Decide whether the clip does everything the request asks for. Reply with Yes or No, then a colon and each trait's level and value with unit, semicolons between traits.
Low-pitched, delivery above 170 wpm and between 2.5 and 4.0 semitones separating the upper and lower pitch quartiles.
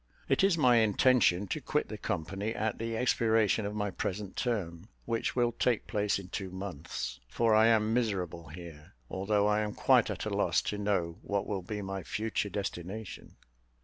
Yes: low, 105 Hz; average, 180 wpm; average, 3.1 semitones